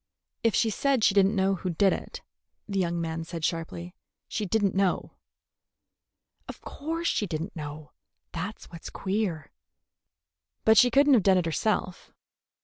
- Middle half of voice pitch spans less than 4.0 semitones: No, average, 4.5 semitones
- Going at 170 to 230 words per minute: Yes, average, 175 wpm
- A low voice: No, high, 190 Hz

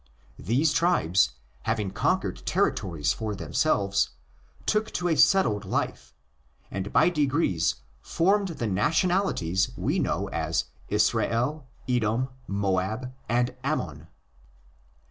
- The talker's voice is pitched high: No, low, 115 Hz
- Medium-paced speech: No, slow, 105 wpm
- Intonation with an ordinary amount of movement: No, wide, 8.2 semitones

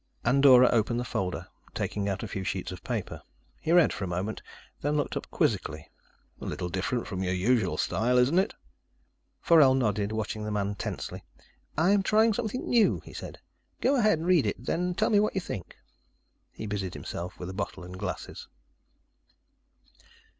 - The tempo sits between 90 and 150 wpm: No, average, 175 wpm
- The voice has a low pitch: Yes, low, 120 Hz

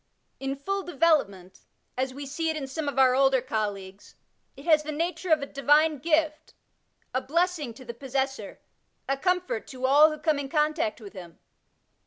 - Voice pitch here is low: No, very high, 280 Hz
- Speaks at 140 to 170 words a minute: No, average, 180 wpm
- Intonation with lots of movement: No, average, 3.4 semitones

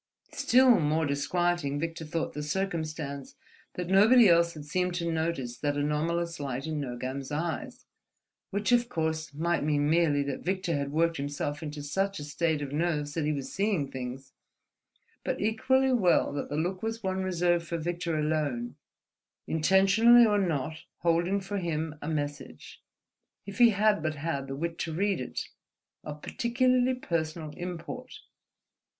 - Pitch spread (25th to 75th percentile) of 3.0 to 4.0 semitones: No, average, 4.4 semitones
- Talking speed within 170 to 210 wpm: No, average, 155 wpm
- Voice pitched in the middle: Yes, medium, 165 Hz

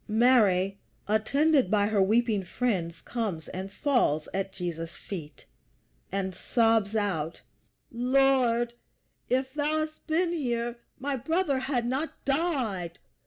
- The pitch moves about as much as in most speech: No, wide, 5.8 semitones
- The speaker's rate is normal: No, slow, 120 wpm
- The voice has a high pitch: Yes, high, 235 Hz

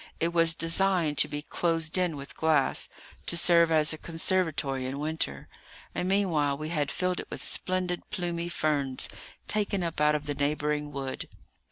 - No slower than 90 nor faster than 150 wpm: No, average, 170 wpm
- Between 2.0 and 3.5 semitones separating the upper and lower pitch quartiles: Yes, average, 2.9 semitones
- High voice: No, medium, 160 Hz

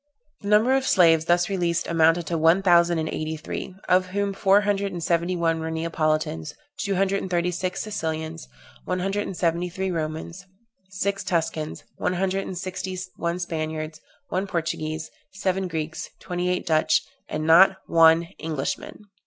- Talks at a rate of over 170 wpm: No, average, 165 wpm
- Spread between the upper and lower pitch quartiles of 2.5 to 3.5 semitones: Yes, average, 2.8 semitones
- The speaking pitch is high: No, medium, 175 Hz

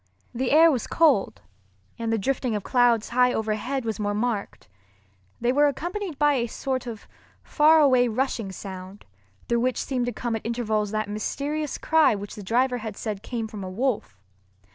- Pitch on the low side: No, high, 240 Hz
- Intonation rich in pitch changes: No, average, 3.9 semitones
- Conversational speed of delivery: Yes, average, 180 wpm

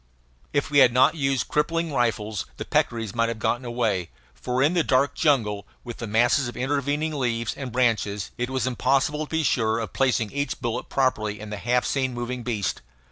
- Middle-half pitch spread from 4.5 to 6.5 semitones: No, average, 3.4 semitones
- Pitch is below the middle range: Yes, low, 125 Hz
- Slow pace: No, average, 195 wpm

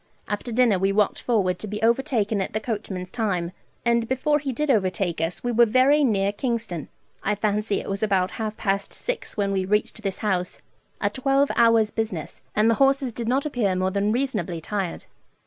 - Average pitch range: Yes, average, 3.6 semitones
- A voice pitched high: Yes, high, 215 Hz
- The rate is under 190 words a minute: No, average, 195 wpm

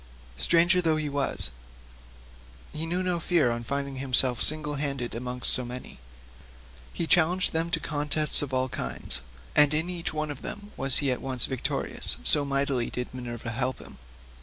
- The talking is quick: No, average, 165 wpm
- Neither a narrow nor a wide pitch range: Yes, average, 4.0 semitones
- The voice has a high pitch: No, medium, 140 Hz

